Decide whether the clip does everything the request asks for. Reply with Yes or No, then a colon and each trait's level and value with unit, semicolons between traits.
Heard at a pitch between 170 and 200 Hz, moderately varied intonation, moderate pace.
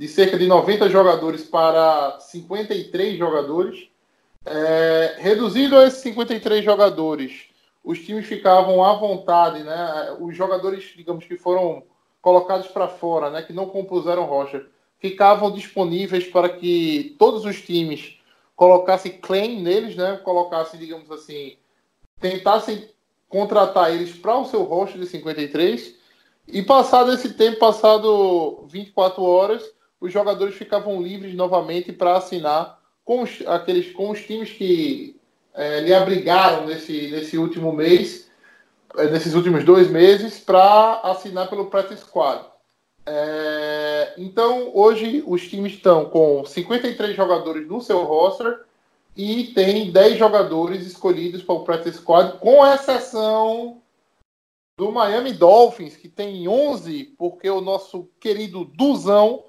Yes: high, 190 Hz; average, 3.8 semitones; average, 130 wpm